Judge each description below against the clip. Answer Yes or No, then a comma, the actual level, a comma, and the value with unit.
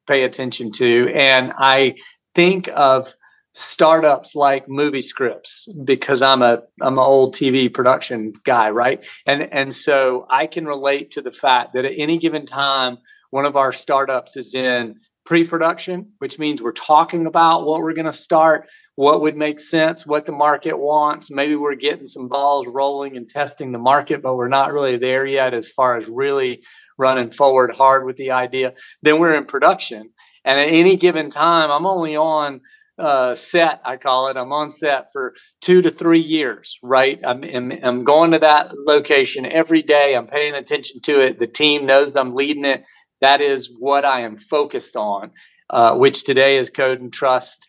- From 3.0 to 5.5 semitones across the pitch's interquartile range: Yes, average, 3.4 semitones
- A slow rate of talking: No, average, 185 wpm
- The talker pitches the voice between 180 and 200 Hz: No, medium, 140 Hz